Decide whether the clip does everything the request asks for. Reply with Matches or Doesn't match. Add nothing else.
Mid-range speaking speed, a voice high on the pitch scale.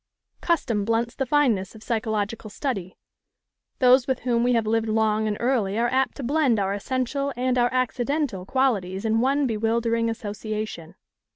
Matches